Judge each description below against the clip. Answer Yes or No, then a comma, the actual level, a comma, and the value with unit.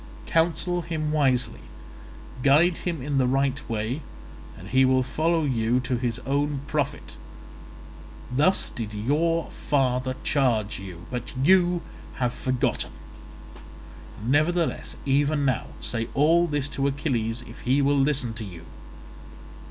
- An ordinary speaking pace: No, slow, 130 wpm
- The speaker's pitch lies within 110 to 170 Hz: Yes, low, 135 Hz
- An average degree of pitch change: Yes, average, 3.6 semitones